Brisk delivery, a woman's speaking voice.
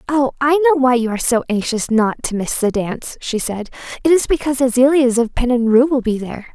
Yes: fast, 220 wpm; female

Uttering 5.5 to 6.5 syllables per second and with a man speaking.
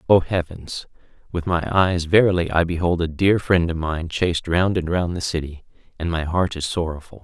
No: 5.1 syllables/s; male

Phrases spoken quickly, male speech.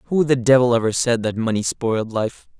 Yes: fast, 210 wpm; male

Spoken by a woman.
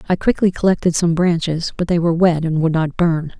Yes: female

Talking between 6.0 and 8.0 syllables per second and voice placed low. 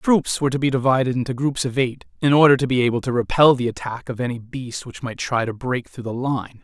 Yes: 6.1 syllables/s; low, 130 Hz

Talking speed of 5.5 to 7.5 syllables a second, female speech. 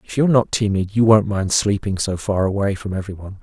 No: 6.3 syllables/s; male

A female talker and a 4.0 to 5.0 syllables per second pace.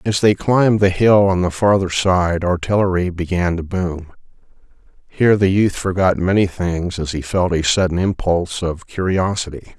No: male; 4.9 syllables/s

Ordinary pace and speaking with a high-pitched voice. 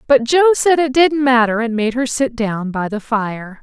No: fast, 230 wpm; high, 245 Hz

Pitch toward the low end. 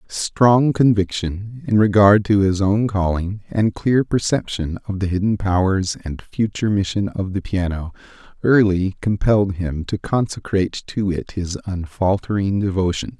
Yes: low, 100 Hz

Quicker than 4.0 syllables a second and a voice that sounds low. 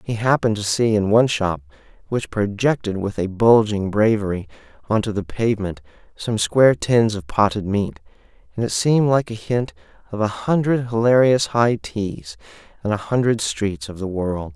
Yes: 5.0 syllables/s; low, 105 Hz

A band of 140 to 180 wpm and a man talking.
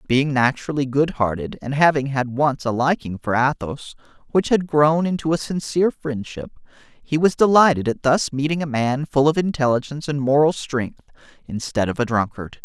Yes: average, 170 wpm; male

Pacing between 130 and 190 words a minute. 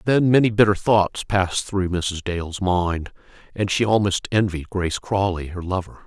Yes: average, 170 wpm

